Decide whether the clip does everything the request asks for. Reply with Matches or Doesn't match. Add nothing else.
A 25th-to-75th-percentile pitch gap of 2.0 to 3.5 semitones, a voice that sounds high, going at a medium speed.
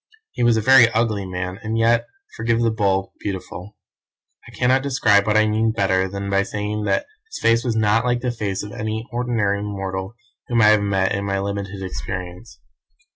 Doesn't match